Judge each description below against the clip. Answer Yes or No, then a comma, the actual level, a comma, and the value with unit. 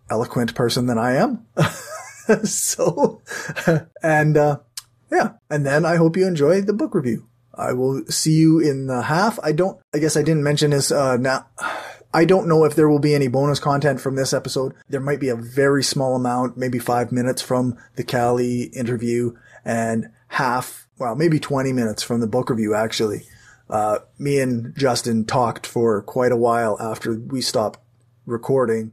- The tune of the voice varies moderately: Yes, average, 3.7 semitones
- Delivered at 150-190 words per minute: Yes, average, 180 wpm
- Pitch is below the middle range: Yes, low, 130 Hz